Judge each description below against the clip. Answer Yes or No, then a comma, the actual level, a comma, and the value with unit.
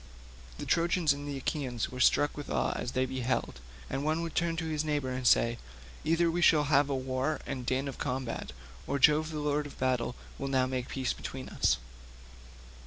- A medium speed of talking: Yes, average, 190 wpm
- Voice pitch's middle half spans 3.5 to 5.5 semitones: No, average, 2.9 semitones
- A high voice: No, medium, 140 Hz